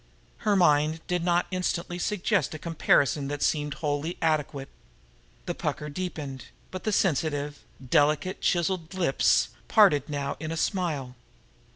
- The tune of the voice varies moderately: Yes, average, 3.6 semitones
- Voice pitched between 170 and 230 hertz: No, medium, 155 Hz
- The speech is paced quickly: No, slow, 135 wpm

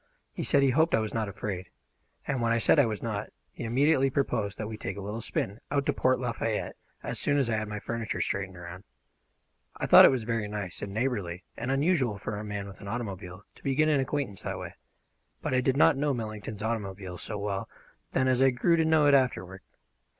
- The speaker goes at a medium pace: No, fast, 225 wpm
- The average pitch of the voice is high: No, low, 115 Hz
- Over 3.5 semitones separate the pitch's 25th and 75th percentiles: Yes, average, 4.7 semitones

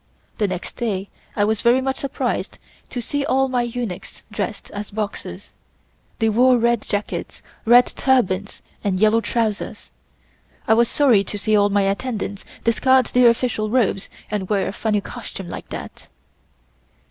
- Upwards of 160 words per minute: No, average, 155 wpm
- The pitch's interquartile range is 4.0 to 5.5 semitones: No, average, 3.3 semitones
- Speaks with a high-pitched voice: Yes, high, 220 Hz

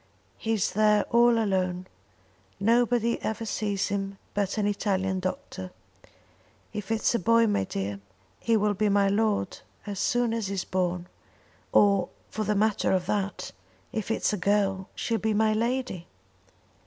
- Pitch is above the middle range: Yes, high, 205 Hz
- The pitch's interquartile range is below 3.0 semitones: Yes, narrow, 2.5 semitones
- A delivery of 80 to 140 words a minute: No, average, 155 wpm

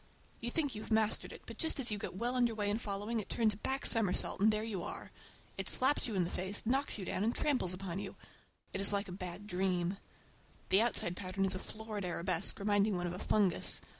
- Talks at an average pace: No, fast, 240 wpm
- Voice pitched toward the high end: Yes, high, 205 Hz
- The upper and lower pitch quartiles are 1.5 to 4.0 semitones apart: Yes, average, 3.3 semitones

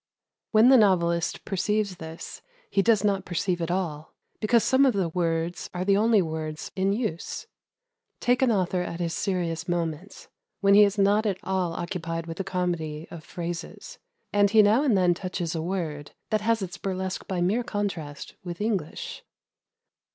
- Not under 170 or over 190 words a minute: Yes, average, 175 wpm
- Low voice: No, medium, 185 Hz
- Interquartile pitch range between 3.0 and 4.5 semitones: Yes, average, 3.4 semitones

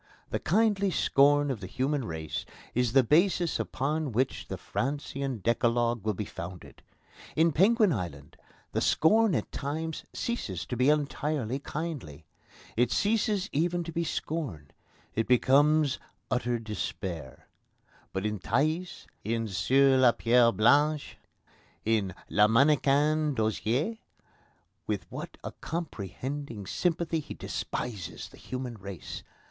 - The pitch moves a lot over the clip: Yes, wide, 6.0 semitones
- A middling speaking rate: No, slow, 125 wpm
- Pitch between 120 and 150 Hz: Yes, low, 135 Hz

